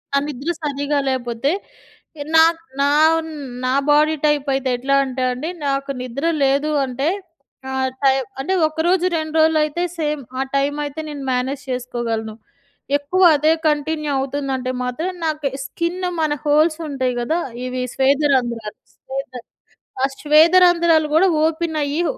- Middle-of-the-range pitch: No, very high, 285 Hz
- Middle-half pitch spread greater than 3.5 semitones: No, average, 2.9 semitones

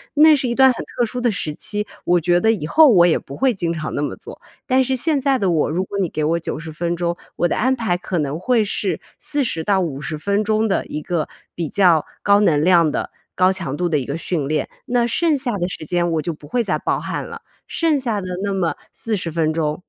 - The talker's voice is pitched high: No, medium, 180 Hz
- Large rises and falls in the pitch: Yes, wide, 6.5 semitones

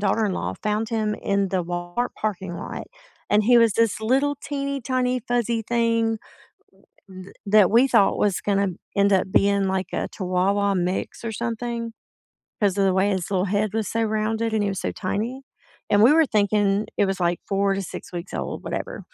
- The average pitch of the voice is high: Yes, high, 210 Hz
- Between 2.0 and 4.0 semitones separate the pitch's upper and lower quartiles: Yes, average, 2.9 semitones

